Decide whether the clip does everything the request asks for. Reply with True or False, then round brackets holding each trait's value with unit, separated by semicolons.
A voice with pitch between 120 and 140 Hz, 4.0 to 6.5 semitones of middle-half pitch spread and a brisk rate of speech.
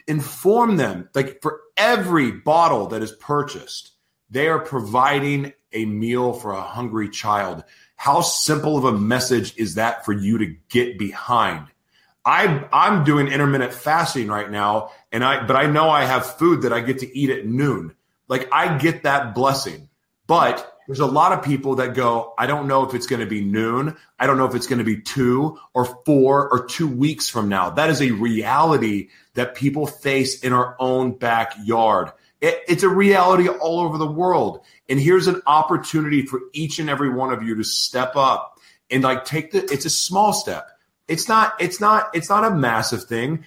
False (135 Hz; 4.6 semitones; 190 wpm)